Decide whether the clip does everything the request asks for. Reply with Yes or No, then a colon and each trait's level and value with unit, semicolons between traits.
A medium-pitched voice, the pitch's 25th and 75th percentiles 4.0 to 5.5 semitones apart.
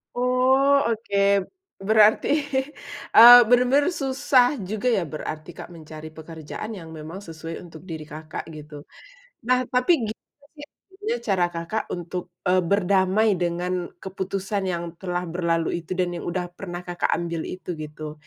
Yes: medium, 180 Hz; average, 5.0 semitones